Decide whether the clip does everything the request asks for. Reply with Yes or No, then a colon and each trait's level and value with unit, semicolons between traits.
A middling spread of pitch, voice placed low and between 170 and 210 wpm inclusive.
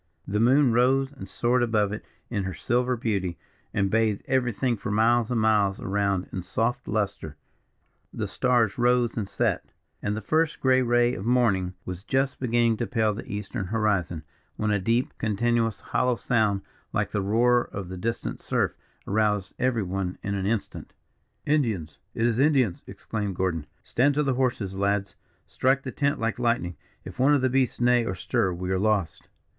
Yes: average, 3.8 semitones; low, 110 Hz; average, 180 wpm